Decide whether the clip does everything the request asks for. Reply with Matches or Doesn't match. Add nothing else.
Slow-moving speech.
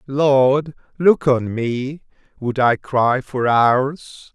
Matches